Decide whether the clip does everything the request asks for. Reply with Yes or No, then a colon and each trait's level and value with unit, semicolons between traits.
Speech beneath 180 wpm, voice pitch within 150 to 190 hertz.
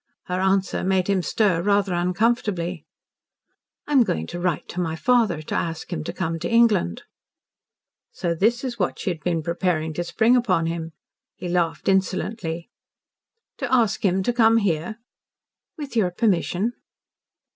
Yes: average, 155 wpm; medium, 185 Hz